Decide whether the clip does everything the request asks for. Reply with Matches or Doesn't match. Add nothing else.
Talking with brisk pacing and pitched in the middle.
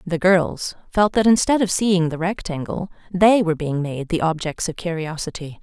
Doesn't match